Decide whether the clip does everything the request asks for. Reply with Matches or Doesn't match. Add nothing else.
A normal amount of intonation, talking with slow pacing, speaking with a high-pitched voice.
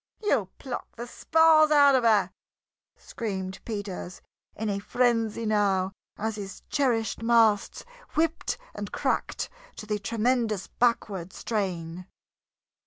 Matches